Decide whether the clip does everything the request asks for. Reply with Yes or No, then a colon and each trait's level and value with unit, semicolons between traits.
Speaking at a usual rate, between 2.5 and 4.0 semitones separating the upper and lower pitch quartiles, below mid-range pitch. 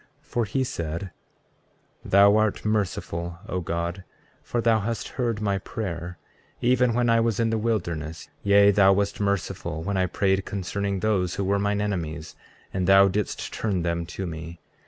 Yes: average, 170 wpm; average, 3.6 semitones; low, 100 Hz